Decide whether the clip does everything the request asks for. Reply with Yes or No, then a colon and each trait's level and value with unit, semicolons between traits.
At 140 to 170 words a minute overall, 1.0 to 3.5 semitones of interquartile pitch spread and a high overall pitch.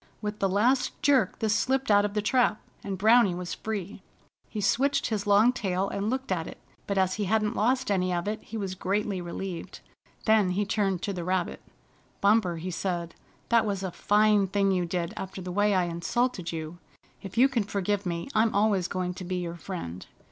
No: fast, 205 wpm; average, 2.9 semitones; high, 200 Hz